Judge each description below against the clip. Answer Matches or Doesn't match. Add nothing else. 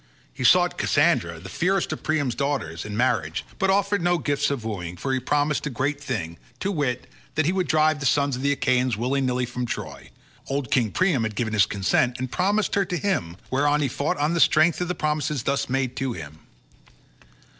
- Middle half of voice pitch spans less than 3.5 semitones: Doesn't match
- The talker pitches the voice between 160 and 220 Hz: Doesn't match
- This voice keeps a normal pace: Doesn't match